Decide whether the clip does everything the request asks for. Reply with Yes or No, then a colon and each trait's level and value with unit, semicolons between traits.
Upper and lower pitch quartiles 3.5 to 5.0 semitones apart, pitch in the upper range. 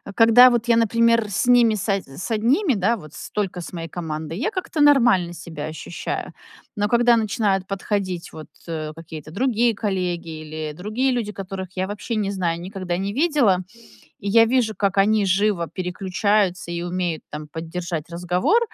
Yes: average, 4.7 semitones; high, 195 Hz